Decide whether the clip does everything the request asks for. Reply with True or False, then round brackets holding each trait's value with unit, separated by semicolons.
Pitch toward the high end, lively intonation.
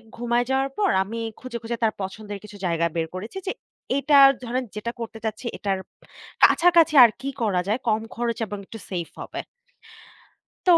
False (230 Hz; 3.8 semitones)